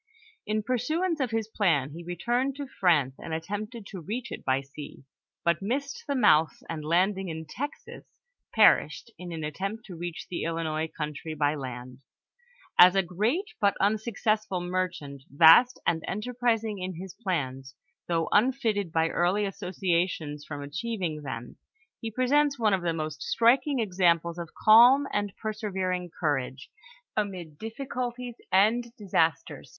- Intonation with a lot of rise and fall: Yes, wide, 5.7 semitones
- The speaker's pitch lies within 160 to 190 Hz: Yes, medium, 185 Hz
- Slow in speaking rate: No, average, 145 wpm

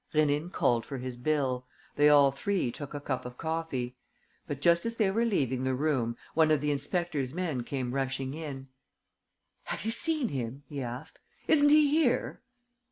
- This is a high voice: No, medium, 145 Hz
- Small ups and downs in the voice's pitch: No, average, 4.8 semitones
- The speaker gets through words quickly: No, average, 175 wpm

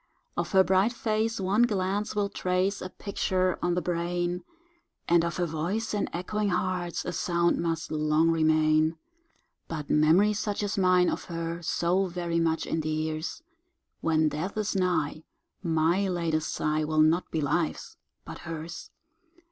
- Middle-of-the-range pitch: Yes, medium, 175 Hz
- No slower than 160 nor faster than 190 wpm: No, average, 150 wpm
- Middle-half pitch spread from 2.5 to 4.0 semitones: Yes, average, 3.0 semitones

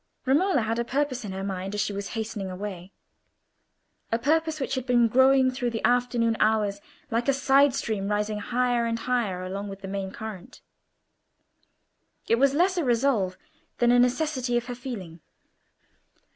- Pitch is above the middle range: Yes, high, 235 Hz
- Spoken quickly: No, average, 170 wpm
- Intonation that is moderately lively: Yes, average, 4.2 semitones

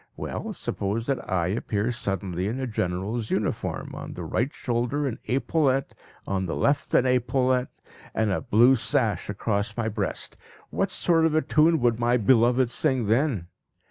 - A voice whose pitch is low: Yes, low, 120 Hz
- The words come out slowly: No, average, 165 wpm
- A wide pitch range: No, average, 4.3 semitones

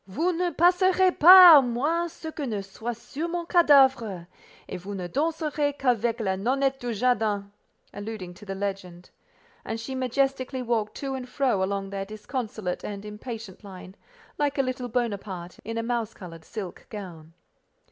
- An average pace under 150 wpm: No, average, 165 wpm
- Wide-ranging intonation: Yes, wide, 5.7 semitones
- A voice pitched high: Yes, high, 235 Hz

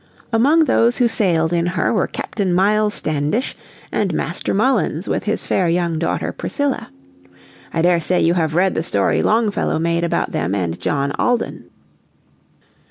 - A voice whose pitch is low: No, medium, 175 Hz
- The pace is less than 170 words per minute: Yes, average, 155 wpm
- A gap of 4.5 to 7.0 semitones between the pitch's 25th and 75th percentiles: Yes, average, 4.8 semitones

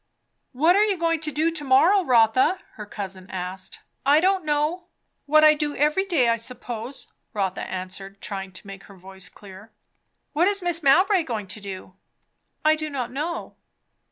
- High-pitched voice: Yes, very high, 270 Hz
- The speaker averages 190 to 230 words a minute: No, average, 175 wpm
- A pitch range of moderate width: No, wide, 8.4 semitones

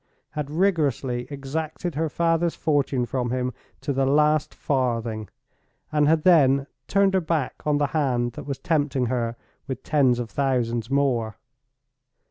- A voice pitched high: No, medium, 140 Hz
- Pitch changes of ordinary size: Yes, average, 3.6 semitones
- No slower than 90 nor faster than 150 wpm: Yes, average, 145 wpm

